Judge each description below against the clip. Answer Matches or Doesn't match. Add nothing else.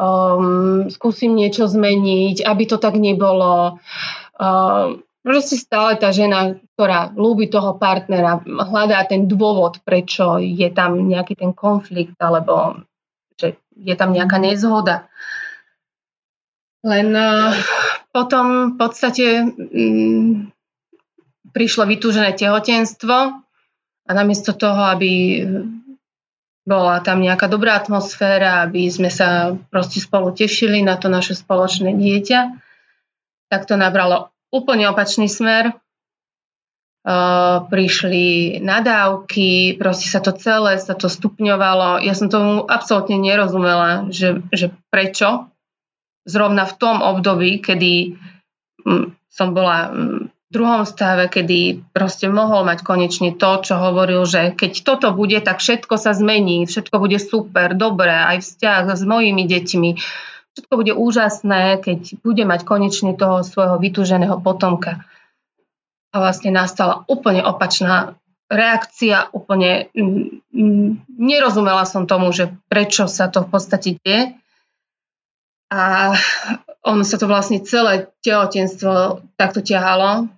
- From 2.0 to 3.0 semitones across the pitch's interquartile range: Matches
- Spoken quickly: Doesn't match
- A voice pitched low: Doesn't match